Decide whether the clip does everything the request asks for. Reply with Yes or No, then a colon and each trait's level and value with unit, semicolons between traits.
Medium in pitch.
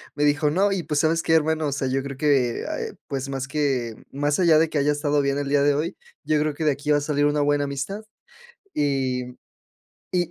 Yes: medium, 145 Hz